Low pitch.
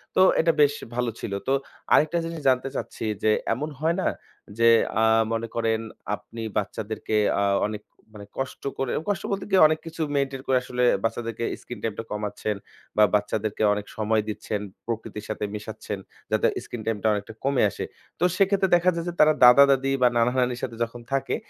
Yes: low, 120 Hz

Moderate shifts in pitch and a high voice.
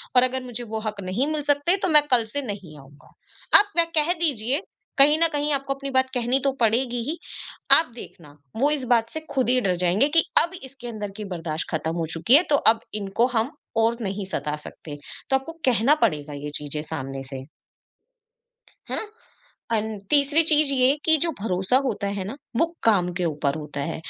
No: wide, 7.5 semitones; high, 235 Hz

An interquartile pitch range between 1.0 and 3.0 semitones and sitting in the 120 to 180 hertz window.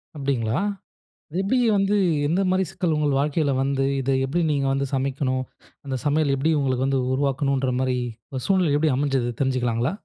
Yes: narrow, 2.5 semitones; medium, 140 Hz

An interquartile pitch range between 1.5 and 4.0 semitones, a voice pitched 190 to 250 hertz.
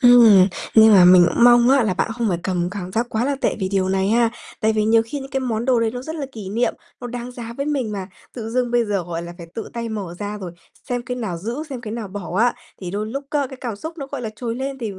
Yes: average, 3.7 semitones; high, 225 Hz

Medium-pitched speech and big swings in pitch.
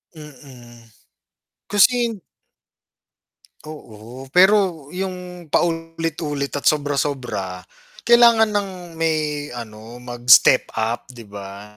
Yes: medium, 145 Hz; wide, 6.5 semitones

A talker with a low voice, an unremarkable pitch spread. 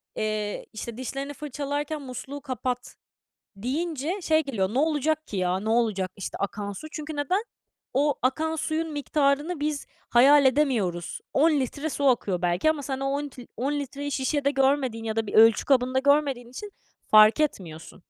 No: very high, 270 Hz; average, 4.6 semitones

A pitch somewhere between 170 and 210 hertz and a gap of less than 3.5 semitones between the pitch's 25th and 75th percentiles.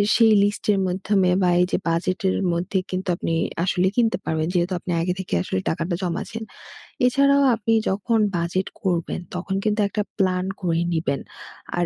Yes: medium, 185 Hz; average, 3.1 semitones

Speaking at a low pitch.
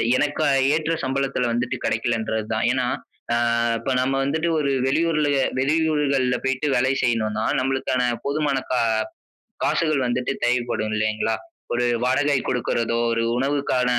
Yes: low, 130 Hz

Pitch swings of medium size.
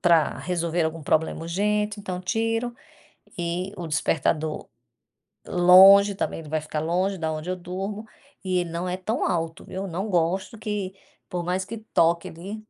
Yes: average, 3.0 semitones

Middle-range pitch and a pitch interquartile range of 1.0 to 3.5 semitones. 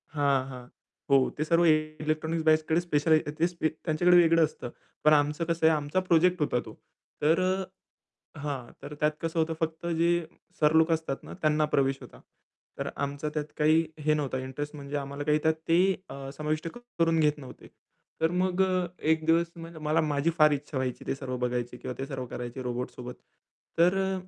Yes: medium, 155 Hz; narrow, 2.6 semitones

